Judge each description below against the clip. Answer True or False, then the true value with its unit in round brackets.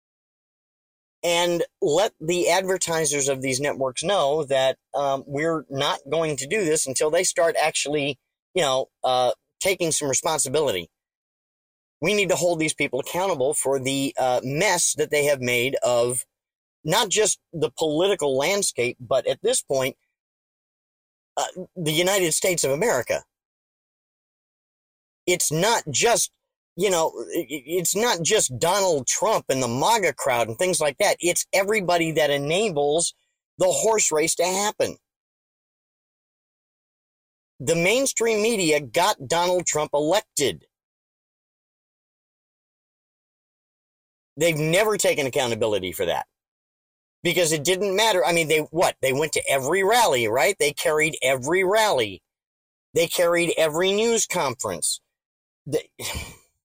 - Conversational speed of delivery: False (130 wpm)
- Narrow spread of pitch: False (5.0 semitones)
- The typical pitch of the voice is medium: True (165 Hz)